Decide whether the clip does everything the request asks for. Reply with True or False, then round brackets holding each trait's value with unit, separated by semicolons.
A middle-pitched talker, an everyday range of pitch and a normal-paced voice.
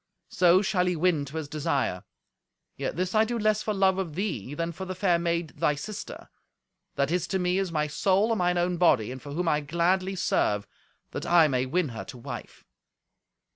False (175 Hz; 4.0 semitones; 210 wpm)